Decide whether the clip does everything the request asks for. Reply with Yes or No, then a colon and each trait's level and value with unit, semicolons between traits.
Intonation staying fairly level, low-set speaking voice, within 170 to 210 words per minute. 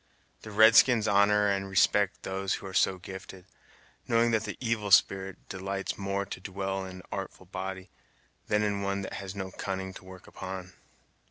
Yes: narrow, 1.3 semitones; very low, 95 Hz; average, 180 wpm